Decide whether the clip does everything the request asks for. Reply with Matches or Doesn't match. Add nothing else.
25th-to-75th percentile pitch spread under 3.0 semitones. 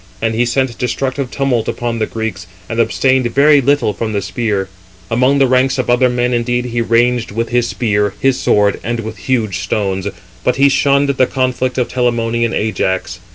Matches